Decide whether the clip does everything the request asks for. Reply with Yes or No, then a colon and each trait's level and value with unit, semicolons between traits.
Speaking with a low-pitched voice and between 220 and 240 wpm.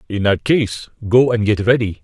No: low, 110 Hz; fast, 205 wpm